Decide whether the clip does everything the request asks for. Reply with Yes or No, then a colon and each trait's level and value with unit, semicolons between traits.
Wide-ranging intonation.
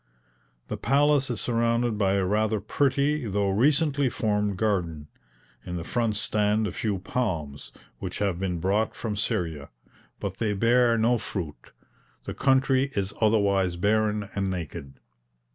No: average, 3.7 semitones